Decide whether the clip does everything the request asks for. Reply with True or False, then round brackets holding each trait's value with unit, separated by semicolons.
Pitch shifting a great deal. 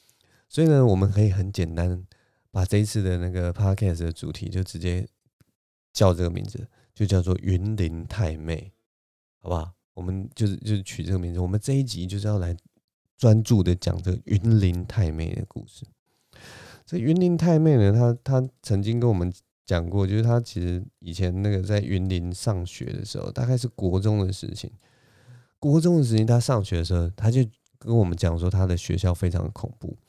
False (4.6 semitones)